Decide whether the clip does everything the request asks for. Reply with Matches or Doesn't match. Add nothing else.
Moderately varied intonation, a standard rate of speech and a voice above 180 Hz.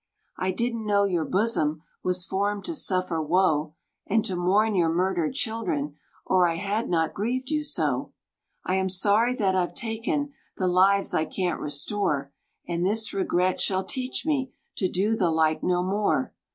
Matches